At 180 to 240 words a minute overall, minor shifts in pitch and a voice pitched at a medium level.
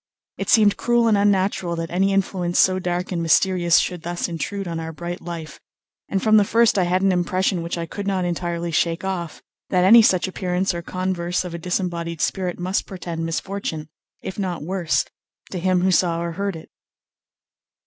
Yes: average, 190 wpm; narrow, 2.1 semitones; medium, 180 Hz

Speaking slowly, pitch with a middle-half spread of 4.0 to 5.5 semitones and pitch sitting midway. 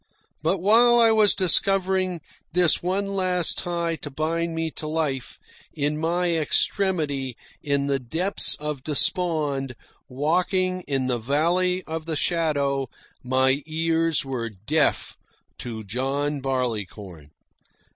Yes: slow, 120 wpm; average, 4.9 semitones; medium, 155 Hz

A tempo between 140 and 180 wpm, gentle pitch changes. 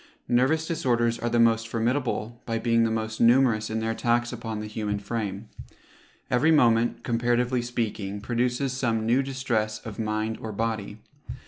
Yes: average, 155 wpm; narrow, 1.8 semitones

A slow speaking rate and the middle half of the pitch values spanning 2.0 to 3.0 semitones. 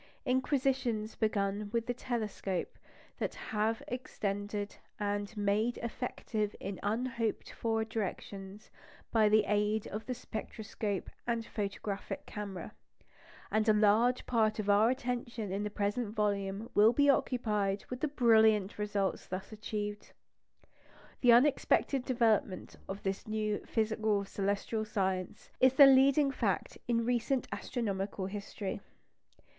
Yes: slow, 125 wpm; narrow, 2.6 semitones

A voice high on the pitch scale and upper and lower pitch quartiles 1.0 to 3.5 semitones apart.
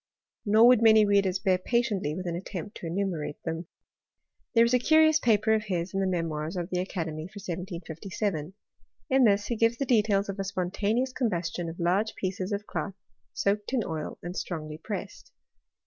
No: high, 195 Hz; average, 4.0 semitones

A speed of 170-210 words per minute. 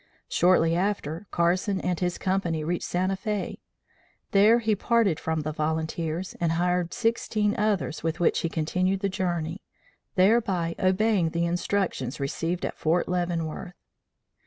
No: slow, 135 wpm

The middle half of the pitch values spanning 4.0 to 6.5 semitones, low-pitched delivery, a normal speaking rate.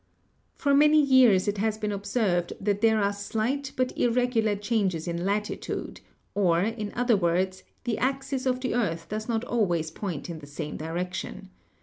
No: average, 4.9 semitones; high, 210 Hz; average, 165 wpm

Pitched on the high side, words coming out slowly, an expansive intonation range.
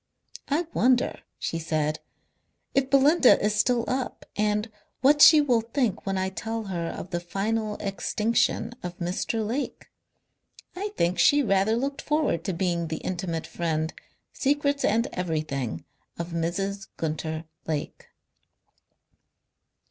Yes: high, 200 Hz; slow, 130 wpm; wide, 6.6 semitones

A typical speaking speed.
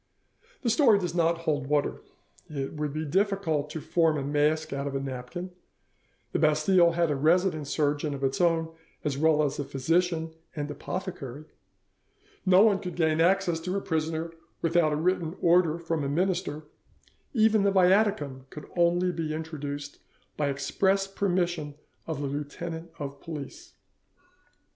Yes: average, 160 wpm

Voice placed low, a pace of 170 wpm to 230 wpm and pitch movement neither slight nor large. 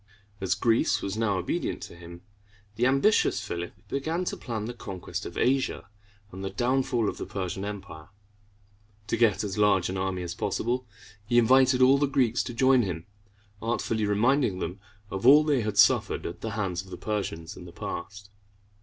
Yes: low, 105 Hz; average, 180 wpm; average, 4.8 semitones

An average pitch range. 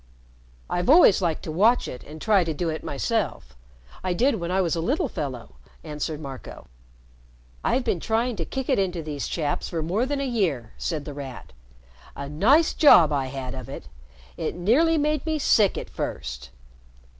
No: wide, 8.4 semitones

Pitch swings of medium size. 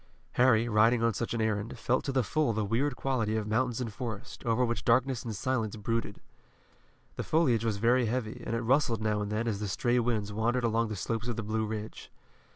No: narrow, 2.2 semitones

